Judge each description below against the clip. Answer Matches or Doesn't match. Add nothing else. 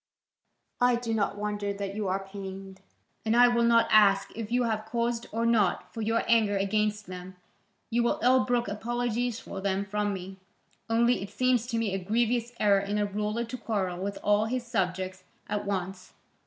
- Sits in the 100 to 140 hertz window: Doesn't match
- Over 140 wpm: Matches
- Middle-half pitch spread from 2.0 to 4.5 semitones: Matches